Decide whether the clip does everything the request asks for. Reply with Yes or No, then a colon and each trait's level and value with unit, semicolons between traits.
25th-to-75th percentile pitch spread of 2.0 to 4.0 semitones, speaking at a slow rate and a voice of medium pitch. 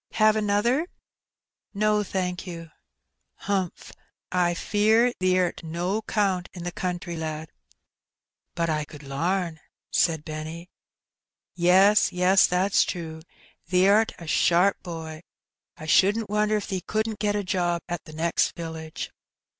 Yes: average, 3.5 semitones; slow, 130 wpm; medium, 180 Hz